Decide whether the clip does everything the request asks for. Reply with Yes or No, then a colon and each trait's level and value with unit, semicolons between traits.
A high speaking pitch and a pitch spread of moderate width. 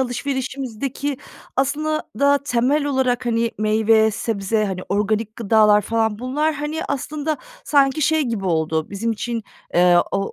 Yes: high, 235 Hz; average, 4.7 semitones